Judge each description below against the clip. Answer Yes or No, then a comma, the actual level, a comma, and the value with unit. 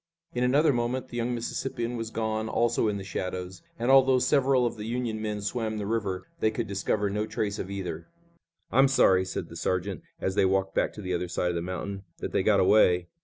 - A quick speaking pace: Yes, fast, 220 wpm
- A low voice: Yes, low, 105 Hz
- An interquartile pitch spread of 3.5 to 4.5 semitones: Yes, average, 4.0 semitones